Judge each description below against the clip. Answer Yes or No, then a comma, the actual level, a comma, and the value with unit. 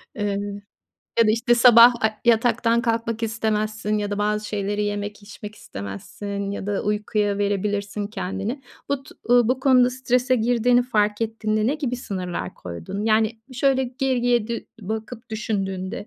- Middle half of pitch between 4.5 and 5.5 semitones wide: No, average, 2.7 semitones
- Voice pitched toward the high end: Yes, high, 215 Hz